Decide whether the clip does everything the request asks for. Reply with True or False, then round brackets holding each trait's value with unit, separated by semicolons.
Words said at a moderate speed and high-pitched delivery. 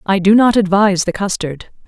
True (190 wpm; 195 Hz)